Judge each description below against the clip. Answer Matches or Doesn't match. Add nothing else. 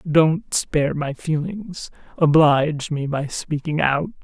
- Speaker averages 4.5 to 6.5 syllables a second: Doesn't match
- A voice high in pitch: Doesn't match